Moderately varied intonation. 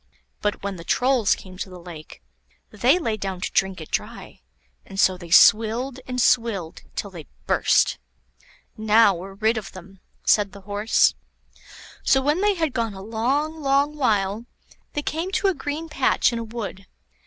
No: wide, 5.7 semitones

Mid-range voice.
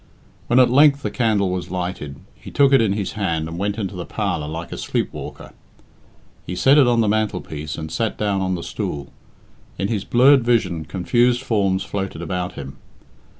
No: low, 100 Hz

